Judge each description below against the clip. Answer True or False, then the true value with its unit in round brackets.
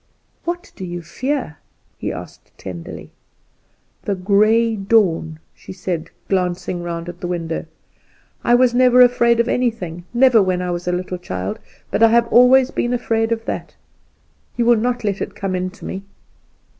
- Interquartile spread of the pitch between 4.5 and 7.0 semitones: True (5.2 semitones)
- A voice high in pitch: True (200 Hz)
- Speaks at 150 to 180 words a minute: True (170 wpm)